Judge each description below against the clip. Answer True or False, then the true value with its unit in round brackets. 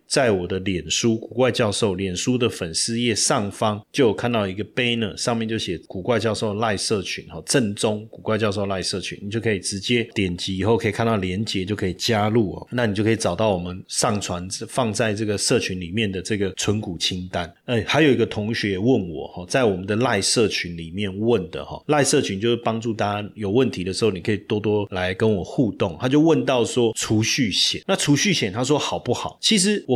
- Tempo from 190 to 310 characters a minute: False (330 characters per minute)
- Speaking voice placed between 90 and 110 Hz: True (105 Hz)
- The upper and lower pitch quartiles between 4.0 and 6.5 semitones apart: False (3.3 semitones)